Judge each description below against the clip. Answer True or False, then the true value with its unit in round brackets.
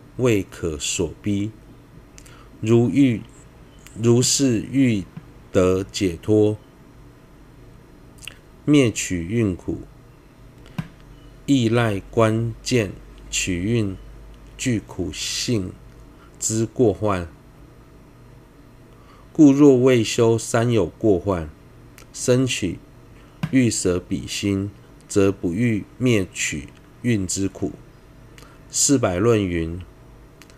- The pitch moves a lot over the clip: False (4.8 semitones)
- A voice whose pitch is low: True (115 Hz)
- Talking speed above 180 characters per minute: False (105 characters per minute)